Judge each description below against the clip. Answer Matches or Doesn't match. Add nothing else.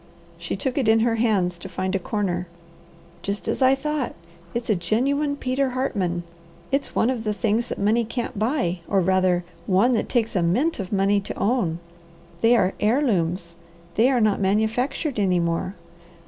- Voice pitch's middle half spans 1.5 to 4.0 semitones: Doesn't match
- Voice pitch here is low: Doesn't match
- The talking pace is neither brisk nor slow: Matches